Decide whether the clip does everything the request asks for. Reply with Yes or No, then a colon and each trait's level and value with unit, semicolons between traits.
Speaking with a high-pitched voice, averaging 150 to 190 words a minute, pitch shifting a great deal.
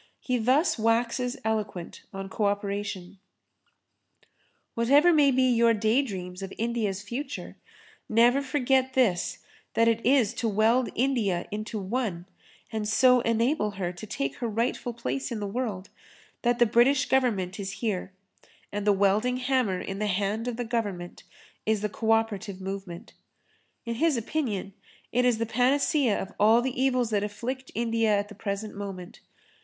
No: high, 225 Hz; average, 155 wpm; average, 3.7 semitones